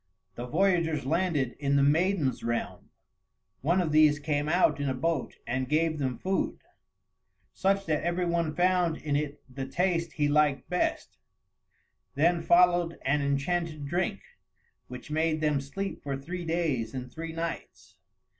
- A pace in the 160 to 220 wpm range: No, average, 150 wpm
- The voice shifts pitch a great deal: No, average, 3.6 semitones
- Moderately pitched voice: Yes, medium, 155 Hz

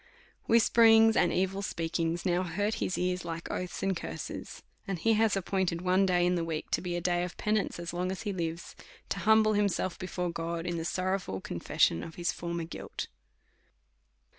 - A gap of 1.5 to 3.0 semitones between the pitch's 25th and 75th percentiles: Yes, narrow, 2.4 semitones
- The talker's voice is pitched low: No, medium, 180 Hz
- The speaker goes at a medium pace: Yes, average, 190 wpm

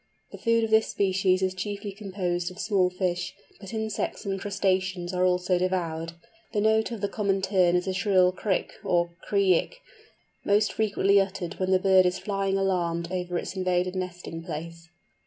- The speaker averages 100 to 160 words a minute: No, average, 175 wpm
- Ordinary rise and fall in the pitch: No, narrow, 1.8 semitones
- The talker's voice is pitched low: No, medium, 185 Hz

